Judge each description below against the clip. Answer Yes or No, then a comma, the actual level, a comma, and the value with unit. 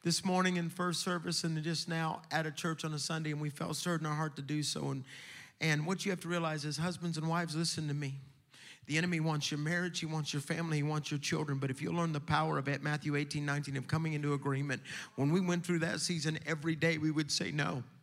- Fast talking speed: Yes, fast, 255 wpm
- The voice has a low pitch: No, medium, 155 Hz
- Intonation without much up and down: Yes, narrow, 2.2 semitones